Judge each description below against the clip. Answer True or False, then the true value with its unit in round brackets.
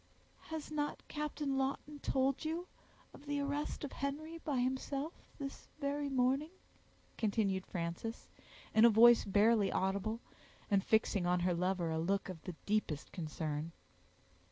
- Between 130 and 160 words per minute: True (140 wpm)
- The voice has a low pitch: False (235 Hz)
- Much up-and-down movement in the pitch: True (7.0 semitones)